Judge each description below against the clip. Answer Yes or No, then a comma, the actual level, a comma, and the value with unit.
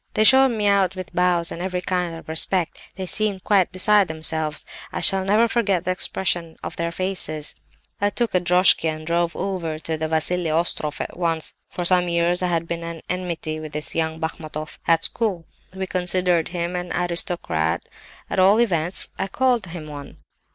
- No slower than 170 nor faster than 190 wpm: Yes, average, 185 wpm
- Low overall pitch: No, medium, 175 Hz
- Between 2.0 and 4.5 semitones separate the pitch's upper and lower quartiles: Yes, narrow, 2.6 semitones